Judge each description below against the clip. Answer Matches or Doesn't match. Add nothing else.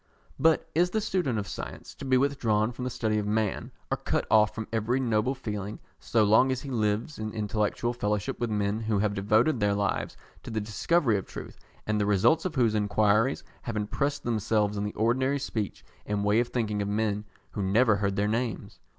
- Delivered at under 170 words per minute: Doesn't match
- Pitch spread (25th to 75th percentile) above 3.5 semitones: Doesn't match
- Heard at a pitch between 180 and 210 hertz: Doesn't match